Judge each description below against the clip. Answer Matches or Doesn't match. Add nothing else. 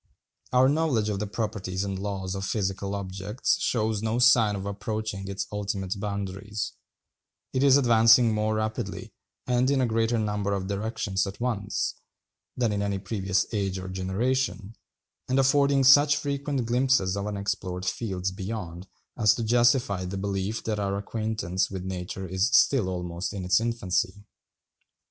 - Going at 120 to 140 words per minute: Doesn't match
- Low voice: Matches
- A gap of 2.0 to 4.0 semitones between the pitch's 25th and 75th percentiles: Matches